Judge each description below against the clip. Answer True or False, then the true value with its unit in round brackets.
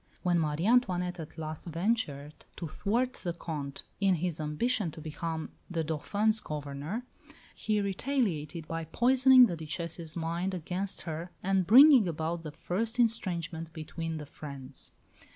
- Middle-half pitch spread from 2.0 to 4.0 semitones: False (4.6 semitones)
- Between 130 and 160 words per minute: True (140 wpm)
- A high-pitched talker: False (170 Hz)